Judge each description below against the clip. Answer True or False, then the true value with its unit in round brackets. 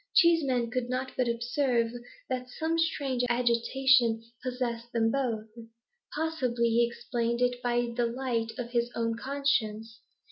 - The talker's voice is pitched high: True (240 Hz)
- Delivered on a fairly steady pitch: True (1.9 semitones)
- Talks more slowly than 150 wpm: True (135 wpm)